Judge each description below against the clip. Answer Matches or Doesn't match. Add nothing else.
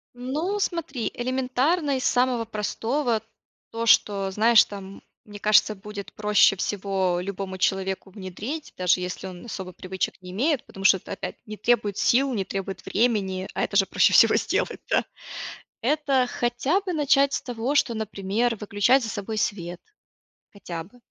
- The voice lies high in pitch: Matches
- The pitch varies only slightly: Doesn't match